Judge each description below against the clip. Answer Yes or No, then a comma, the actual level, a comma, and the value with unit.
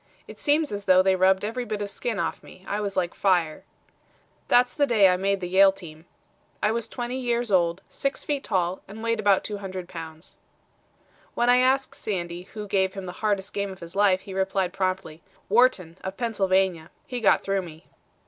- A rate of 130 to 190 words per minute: No, average, 200 wpm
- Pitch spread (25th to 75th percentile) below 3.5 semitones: Yes, average, 3.1 semitones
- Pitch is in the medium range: No, high, 195 Hz